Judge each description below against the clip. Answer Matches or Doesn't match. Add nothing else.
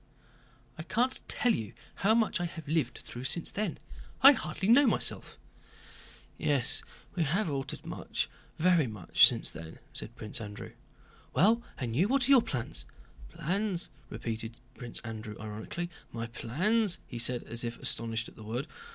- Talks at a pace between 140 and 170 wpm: Matches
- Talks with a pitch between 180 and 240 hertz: Doesn't match